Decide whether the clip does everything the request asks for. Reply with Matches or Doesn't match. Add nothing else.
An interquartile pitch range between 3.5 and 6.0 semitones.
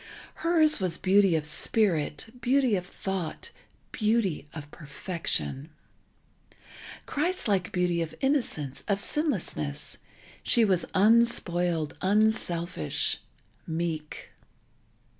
Matches